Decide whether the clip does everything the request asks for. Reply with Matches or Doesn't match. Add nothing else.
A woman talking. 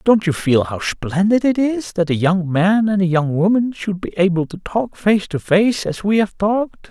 Doesn't match